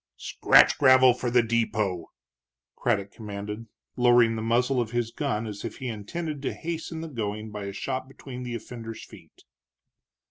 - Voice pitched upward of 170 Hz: No, low, 115 Hz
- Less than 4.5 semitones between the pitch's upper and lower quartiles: Yes, average, 3.3 semitones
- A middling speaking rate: Yes, average, 165 wpm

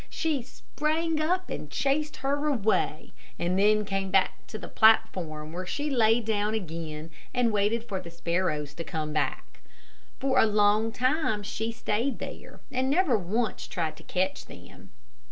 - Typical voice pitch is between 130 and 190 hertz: No, high, 215 Hz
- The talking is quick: No, average, 160 wpm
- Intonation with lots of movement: Yes, wide, 6.2 semitones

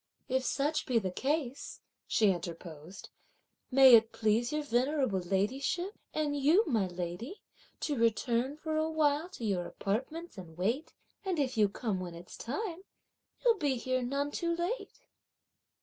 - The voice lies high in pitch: Yes, very high, 260 Hz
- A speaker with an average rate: Yes, average, 150 wpm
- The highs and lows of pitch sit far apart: Yes, wide, 6.9 semitones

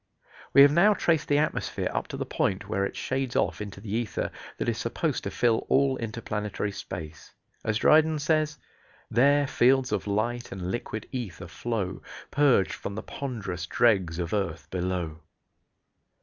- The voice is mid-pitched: No, low, 110 Hz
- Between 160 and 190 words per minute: Yes, average, 165 wpm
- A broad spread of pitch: Yes, wide, 6.1 semitones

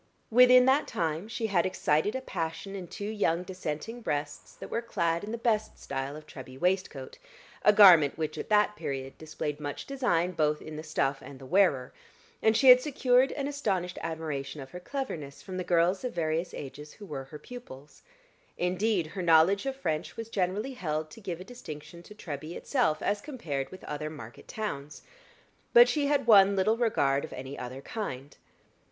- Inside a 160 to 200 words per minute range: Yes, average, 185 wpm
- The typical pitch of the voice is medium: Yes, medium, 175 Hz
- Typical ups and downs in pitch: No, wide, 6.4 semitones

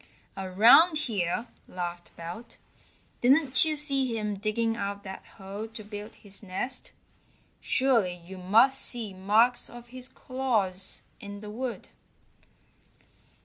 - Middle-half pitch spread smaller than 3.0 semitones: No, average, 4.4 semitones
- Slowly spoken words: Yes, slow, 120 wpm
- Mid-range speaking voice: No, high, 215 Hz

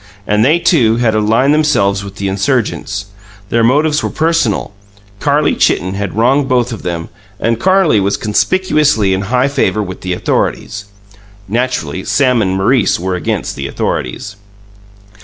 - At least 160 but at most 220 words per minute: No, average, 150 wpm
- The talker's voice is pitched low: Yes, low, 110 Hz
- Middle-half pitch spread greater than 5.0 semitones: Yes, wide, 5.6 semitones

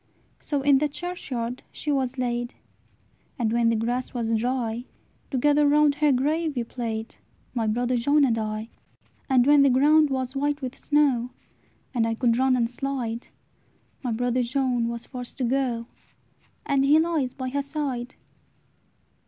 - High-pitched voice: Yes, very high, 255 Hz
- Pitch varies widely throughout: No, average, 3.0 semitones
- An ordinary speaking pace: Yes, average, 160 wpm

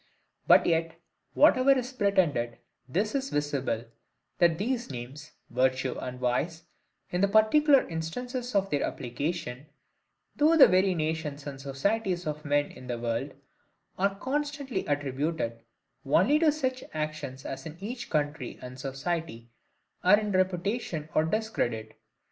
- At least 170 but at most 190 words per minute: No, slow, 135 wpm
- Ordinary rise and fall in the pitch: No, wide, 7.9 semitones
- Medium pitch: Yes, medium, 160 Hz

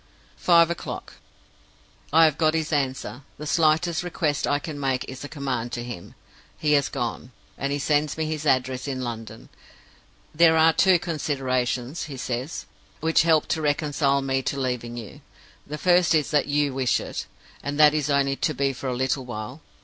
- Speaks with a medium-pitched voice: Yes, medium, 145 Hz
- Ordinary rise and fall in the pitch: Yes, average, 3.2 semitones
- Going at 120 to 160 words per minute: No, average, 185 wpm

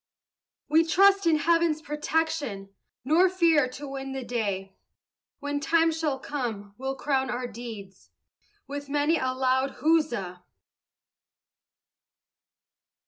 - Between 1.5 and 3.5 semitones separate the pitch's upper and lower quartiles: No, average, 4.7 semitones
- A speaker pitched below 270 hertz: No, very high, 280 Hz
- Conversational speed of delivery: No, slow, 110 wpm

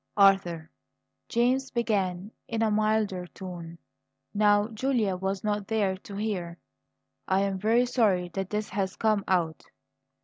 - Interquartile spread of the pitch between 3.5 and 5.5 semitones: No, average, 2.7 semitones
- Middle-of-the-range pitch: No, high, 200 Hz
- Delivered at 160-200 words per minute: No, slow, 135 wpm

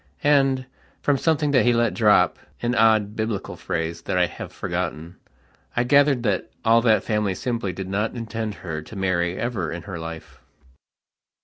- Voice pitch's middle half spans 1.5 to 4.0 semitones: No, average, 5.1 semitones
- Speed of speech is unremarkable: Yes, average, 155 wpm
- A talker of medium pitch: No, low, 105 Hz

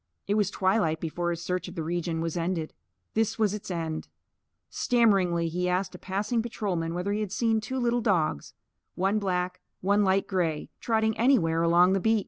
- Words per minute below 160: No, average, 185 wpm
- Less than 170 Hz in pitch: No, medium, 185 Hz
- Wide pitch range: No, average, 3.8 semitones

